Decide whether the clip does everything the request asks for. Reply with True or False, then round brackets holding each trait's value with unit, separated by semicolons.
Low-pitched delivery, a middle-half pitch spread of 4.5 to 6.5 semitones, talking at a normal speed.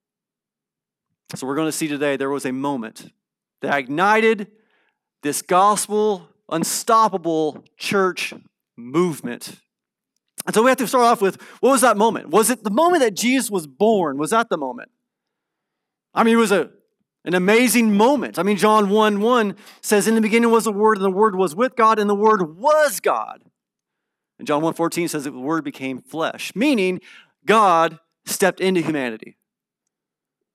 False (205 Hz; 5.6 semitones; 170 wpm)